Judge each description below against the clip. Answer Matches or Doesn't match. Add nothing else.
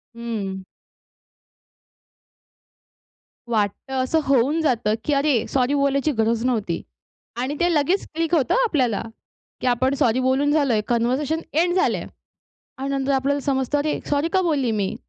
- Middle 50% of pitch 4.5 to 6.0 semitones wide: Doesn't match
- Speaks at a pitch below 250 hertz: Doesn't match